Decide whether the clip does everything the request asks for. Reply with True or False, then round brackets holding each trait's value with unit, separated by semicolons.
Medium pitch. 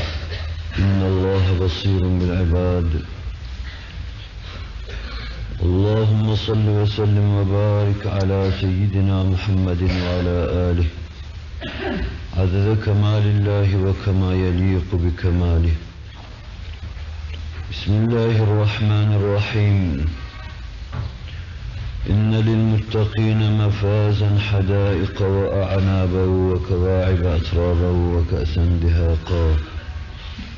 False (95 Hz)